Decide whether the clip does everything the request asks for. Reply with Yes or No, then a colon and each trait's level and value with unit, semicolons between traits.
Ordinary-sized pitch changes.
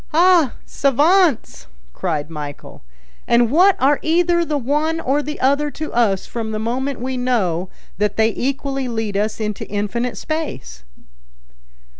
No: wide, 5.7 semitones